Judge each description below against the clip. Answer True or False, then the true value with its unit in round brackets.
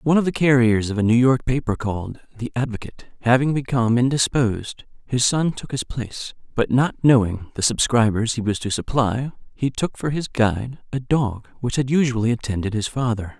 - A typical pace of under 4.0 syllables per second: False (5.5 syllables/s)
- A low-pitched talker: True (120 Hz)